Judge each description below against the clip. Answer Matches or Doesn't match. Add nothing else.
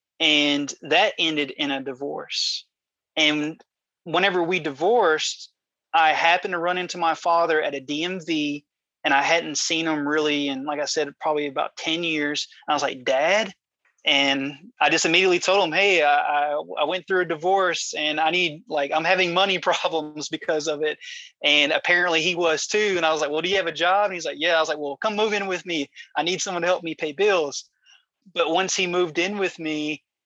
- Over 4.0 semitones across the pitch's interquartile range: Doesn't match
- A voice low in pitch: Doesn't match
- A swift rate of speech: Matches